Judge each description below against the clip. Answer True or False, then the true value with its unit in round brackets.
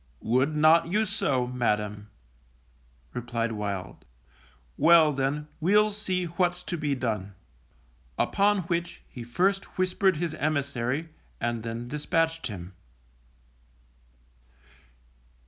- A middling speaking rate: False (100 wpm)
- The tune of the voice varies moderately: False (6.8 semitones)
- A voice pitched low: False (150 Hz)